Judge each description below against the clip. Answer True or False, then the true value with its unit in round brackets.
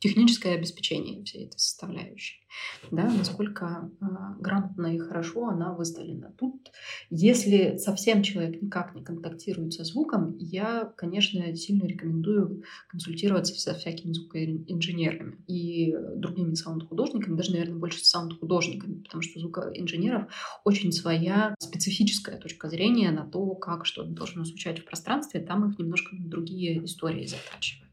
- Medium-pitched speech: True (175 Hz)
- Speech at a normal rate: True (125 wpm)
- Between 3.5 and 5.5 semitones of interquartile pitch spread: False (3.1 semitones)